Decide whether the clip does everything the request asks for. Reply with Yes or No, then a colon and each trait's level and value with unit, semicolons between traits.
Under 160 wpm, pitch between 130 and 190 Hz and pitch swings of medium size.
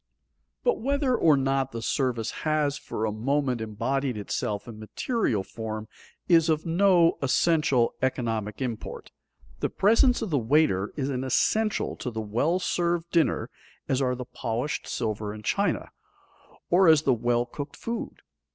No: average, 150 wpm; low, 135 Hz; wide, 6.4 semitones